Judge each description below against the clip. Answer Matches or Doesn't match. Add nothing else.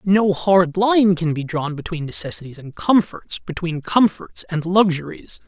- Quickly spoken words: Doesn't match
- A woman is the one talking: Doesn't match